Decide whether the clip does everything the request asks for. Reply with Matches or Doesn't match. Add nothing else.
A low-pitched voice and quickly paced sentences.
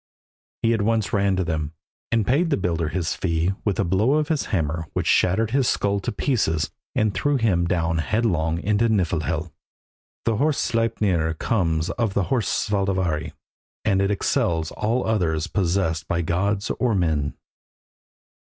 Doesn't match